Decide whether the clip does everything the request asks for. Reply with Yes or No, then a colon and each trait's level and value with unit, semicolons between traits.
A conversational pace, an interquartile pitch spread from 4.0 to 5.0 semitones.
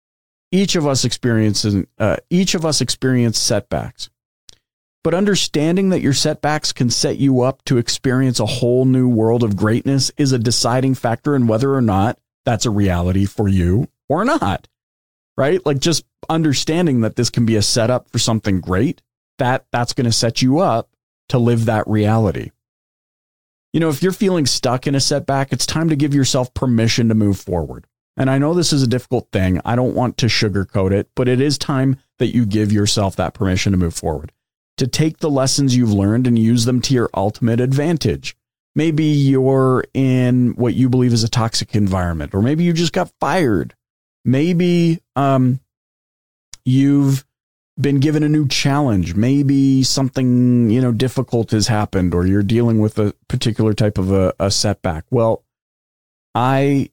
Yes: average, 175 wpm; average, 4.3 semitones